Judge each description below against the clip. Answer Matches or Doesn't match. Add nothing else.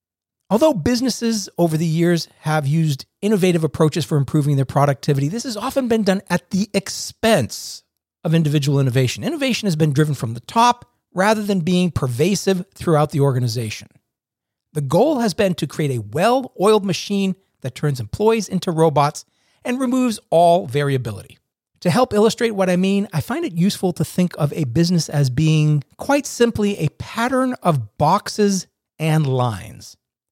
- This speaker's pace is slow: Doesn't match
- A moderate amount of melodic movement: Doesn't match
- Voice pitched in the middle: Matches